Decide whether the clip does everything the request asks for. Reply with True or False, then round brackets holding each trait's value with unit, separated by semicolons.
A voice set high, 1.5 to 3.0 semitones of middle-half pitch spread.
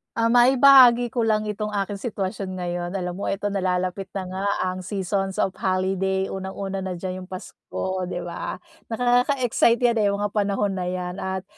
True (195 Hz; 2.4 semitones)